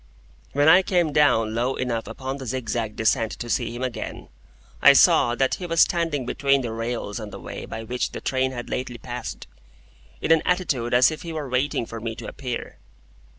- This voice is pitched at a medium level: No, low, 125 Hz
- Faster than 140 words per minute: Yes, average, 200 wpm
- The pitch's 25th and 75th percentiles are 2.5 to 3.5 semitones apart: No, average, 3.9 semitones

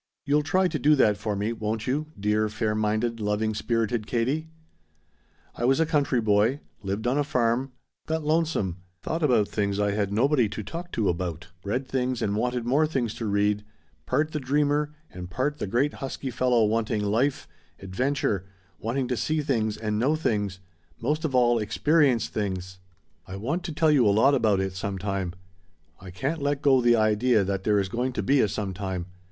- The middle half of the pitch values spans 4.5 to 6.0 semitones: Yes, average, 5.2 semitones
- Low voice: Yes, low, 115 Hz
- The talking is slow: No, average, 190 wpm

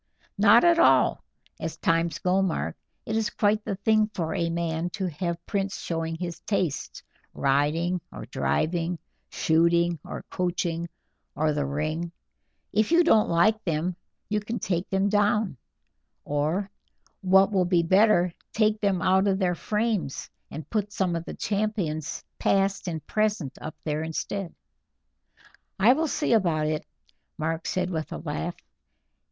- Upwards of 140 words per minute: Yes, average, 150 wpm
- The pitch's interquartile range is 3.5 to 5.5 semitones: Yes, average, 4.0 semitones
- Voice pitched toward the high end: No, medium, 180 Hz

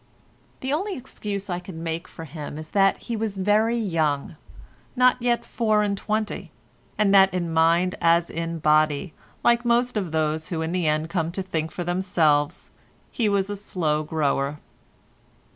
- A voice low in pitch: No, medium, 180 Hz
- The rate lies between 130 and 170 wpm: Yes, average, 160 wpm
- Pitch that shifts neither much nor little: Yes, average, 4.7 semitones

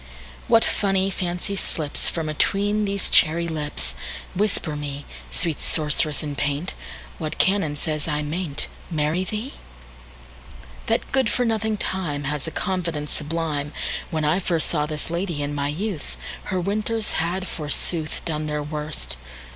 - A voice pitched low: No, medium, 155 Hz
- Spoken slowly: Yes, slow, 115 wpm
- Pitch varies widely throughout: No, average, 4.2 semitones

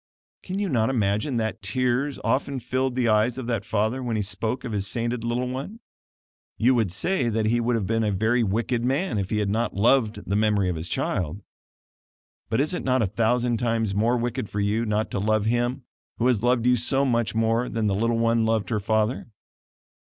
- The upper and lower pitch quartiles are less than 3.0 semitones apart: Yes, narrow, 2.6 semitones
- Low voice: Yes, low, 115 Hz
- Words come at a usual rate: No, fast, 215 wpm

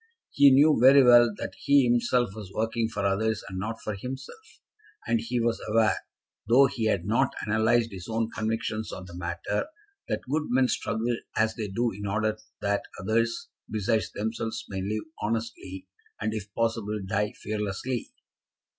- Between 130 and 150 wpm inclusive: No, average, 165 wpm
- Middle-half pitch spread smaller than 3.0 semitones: Yes, narrow, 2.4 semitones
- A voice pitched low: Yes, low, 110 Hz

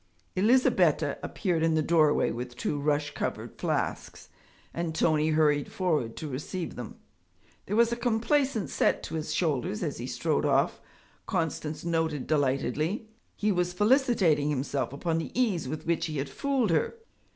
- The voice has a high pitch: No, medium, 160 Hz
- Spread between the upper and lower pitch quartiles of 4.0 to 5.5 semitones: Yes, average, 4.9 semitones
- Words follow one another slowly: No, average, 155 wpm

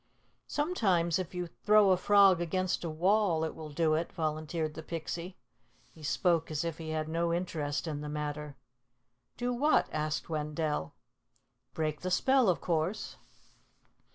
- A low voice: No, medium, 165 Hz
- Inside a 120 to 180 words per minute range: Yes, average, 155 wpm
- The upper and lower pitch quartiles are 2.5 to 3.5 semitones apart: Yes, average, 3.0 semitones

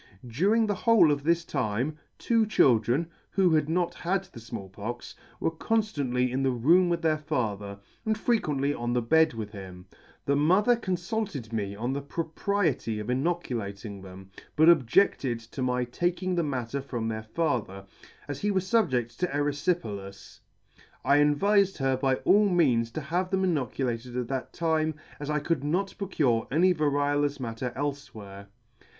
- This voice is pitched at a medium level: Yes, medium, 145 Hz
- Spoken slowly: No, average, 165 wpm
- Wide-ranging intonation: Yes, wide, 6.4 semitones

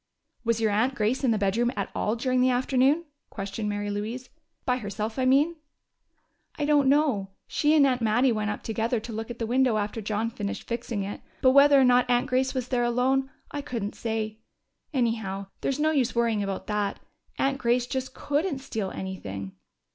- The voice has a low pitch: No, high, 235 Hz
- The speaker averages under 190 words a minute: No, average, 195 wpm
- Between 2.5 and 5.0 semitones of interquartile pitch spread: Yes, average, 3.7 semitones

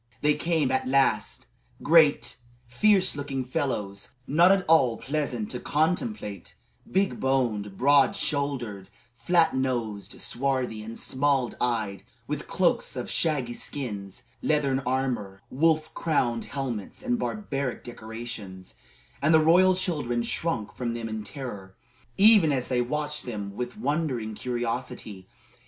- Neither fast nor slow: No, slow, 130 wpm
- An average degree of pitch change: Yes, average, 5.0 semitones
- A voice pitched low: Yes, low, 130 Hz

